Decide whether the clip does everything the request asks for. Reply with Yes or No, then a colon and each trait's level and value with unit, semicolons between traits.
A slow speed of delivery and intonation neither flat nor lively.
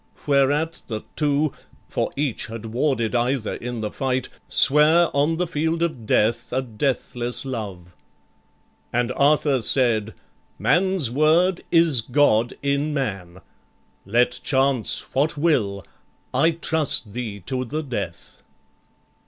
Yes: slow, 120 wpm; average, 4.6 semitones